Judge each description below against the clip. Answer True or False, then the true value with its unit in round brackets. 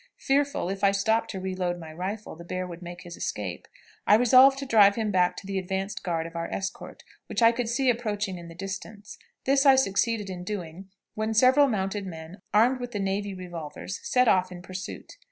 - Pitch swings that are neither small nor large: True (3.9 semitones)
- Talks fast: True (210 wpm)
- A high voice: True (195 Hz)